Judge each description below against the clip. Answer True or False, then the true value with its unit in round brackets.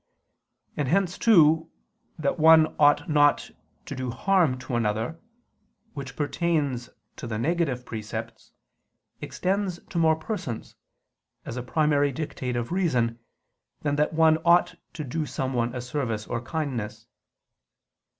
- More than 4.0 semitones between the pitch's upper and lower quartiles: True (4.7 semitones)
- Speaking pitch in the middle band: True (145 Hz)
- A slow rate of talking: True (130 wpm)